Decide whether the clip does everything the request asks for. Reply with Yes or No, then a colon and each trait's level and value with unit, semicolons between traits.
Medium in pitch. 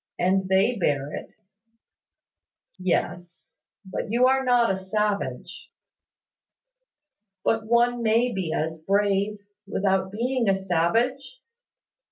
No: high, 200 Hz